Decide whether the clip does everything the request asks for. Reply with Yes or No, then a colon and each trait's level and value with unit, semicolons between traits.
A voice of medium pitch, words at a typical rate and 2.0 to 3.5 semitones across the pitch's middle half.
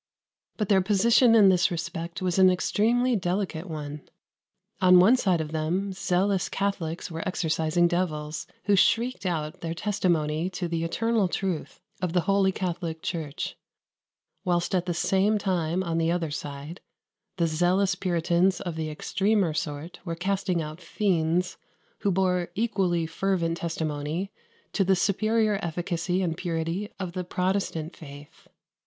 Yes: medium, 180 Hz; average, 145 wpm; average, 2.9 semitones